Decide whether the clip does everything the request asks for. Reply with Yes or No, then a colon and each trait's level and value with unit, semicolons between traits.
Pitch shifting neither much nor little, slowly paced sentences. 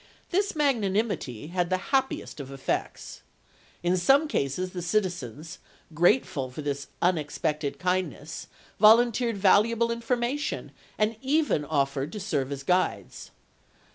No: wide, 7.7 semitones; slow, 115 wpm